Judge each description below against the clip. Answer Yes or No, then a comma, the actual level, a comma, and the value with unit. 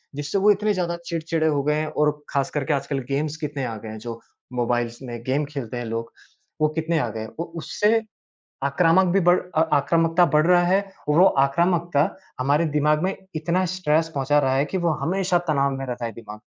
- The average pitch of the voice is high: No, medium, 150 Hz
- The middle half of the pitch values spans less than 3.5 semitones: No, average, 4.2 semitones